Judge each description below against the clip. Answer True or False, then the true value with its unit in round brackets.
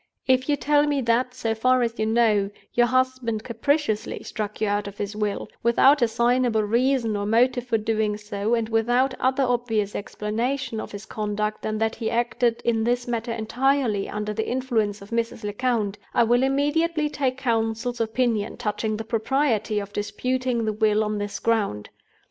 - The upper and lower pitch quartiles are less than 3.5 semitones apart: True (3.0 semitones)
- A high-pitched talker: True (230 Hz)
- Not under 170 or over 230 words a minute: True (175 wpm)